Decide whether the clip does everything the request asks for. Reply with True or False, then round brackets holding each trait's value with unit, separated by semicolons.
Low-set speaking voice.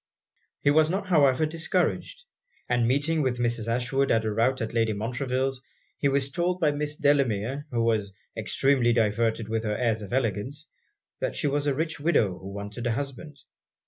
True (130 Hz)